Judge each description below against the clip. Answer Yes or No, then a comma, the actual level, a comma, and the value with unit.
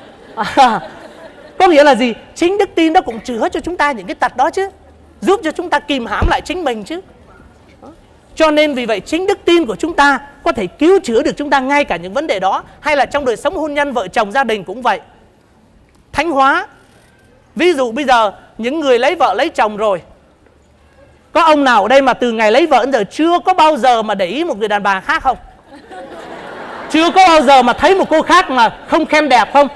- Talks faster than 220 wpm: Yes, average, 235 wpm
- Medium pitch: No, very high, 290 Hz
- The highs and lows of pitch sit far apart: No, average, 4.7 semitones